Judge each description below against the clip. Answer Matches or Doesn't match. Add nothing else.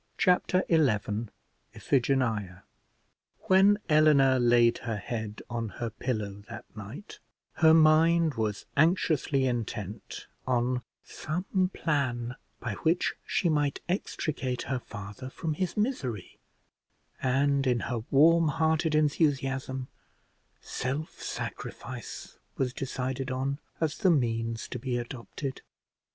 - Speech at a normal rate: Doesn't match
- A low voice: Matches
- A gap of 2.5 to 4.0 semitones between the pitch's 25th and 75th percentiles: Doesn't match